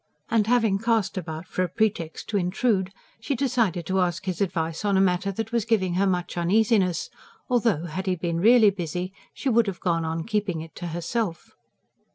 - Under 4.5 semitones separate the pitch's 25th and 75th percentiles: Yes, average, 4.0 semitones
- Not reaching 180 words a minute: No, average, 195 wpm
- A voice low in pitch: No, high, 190 Hz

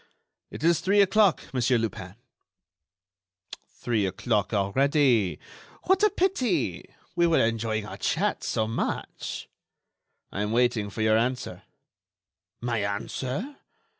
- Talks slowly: Yes, slow, 115 wpm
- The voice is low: Yes, low, 120 Hz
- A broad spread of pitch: Yes, wide, 7.6 semitones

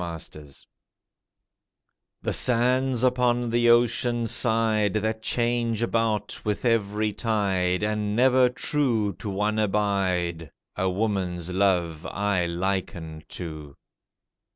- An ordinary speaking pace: No, slow, 105 wpm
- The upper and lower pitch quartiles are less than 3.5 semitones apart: No, average, 4.2 semitones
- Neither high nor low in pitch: No, low, 105 Hz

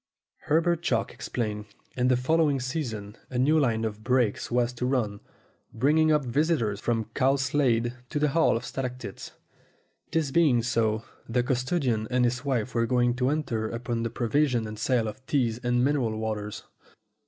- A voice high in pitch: No, low, 125 Hz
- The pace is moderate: Yes, average, 165 wpm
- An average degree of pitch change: Yes, average, 3.3 semitones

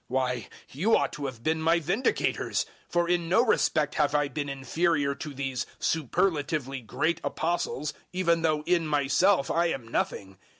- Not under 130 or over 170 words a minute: Yes, average, 160 wpm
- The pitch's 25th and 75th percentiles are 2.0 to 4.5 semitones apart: Yes, average, 3.8 semitones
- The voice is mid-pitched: Yes, medium, 150 Hz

